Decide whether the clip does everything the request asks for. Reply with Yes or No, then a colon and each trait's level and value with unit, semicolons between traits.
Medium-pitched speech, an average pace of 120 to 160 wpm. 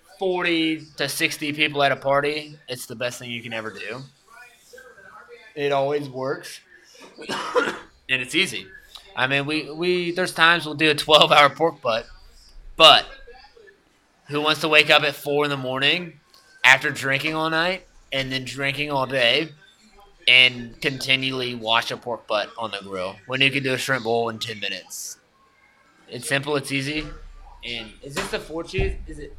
No: medium, 145 Hz; average, 175 wpm